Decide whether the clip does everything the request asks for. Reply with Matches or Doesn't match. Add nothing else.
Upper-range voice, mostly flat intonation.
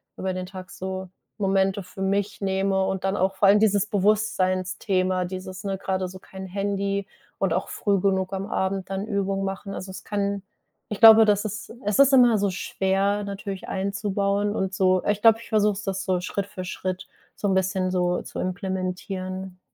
Matches